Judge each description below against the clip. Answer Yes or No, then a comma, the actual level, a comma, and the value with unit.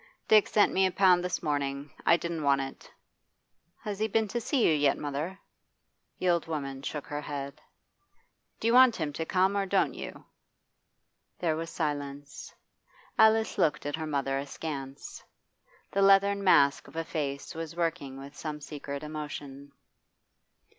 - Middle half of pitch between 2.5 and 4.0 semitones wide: No, average, 5.0 semitones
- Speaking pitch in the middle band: Yes, medium, 155 Hz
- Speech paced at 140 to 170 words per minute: Yes, average, 160 wpm